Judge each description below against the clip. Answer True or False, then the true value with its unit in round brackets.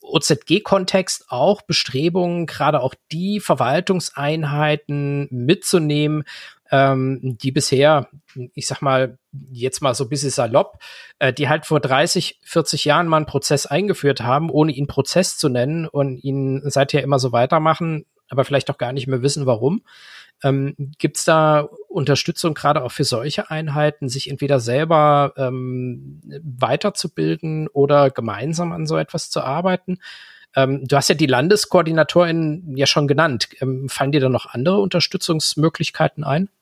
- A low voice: False (145 Hz)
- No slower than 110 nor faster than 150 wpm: True (145 wpm)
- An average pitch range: True (3.3 semitones)